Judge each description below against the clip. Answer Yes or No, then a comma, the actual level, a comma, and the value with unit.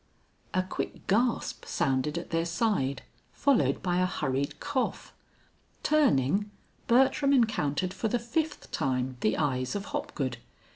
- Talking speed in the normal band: No, slow, 130 wpm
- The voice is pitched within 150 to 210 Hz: Yes, medium, 185 Hz